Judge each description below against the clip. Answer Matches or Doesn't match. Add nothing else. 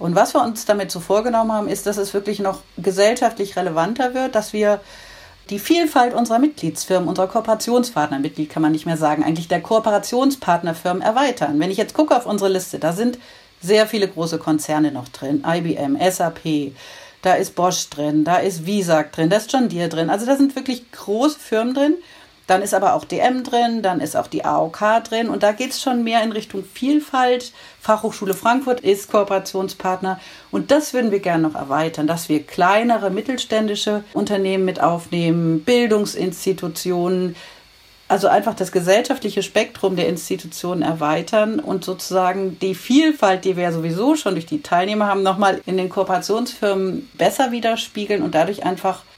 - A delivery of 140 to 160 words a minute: Doesn't match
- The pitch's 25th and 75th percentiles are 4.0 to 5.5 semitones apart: Matches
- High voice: Matches